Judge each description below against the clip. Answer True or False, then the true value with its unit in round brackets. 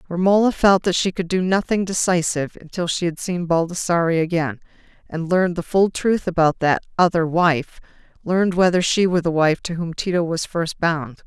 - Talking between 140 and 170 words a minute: False (180 wpm)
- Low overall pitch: False (175 Hz)